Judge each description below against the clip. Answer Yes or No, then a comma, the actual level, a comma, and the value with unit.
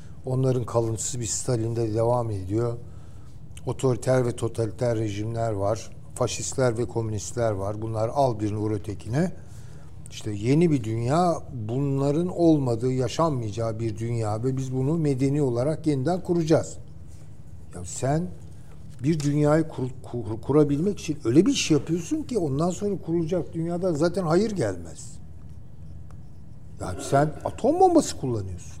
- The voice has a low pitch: Yes, low, 125 Hz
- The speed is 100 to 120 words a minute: No, average, 135 wpm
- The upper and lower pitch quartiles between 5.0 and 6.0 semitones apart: Yes, average, 5.3 semitones